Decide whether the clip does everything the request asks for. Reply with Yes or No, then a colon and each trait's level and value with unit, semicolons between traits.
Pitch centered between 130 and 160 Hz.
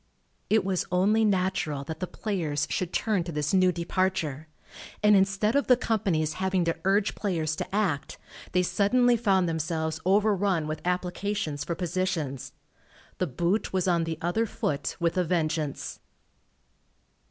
No: medium, 180 Hz